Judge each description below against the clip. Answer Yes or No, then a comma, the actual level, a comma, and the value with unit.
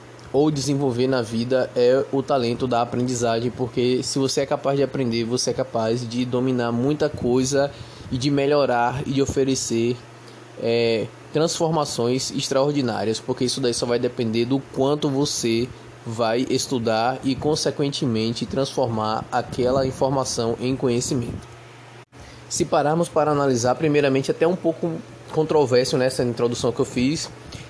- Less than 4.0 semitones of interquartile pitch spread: Yes, average, 2.7 semitones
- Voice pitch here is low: Yes, low, 130 Hz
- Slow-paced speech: No, average, 140 wpm